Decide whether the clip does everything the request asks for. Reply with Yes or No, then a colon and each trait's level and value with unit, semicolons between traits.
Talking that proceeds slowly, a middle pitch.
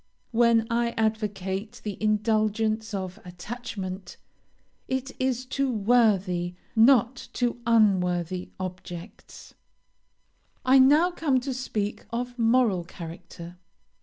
No: slow, 100 wpm; high, 220 Hz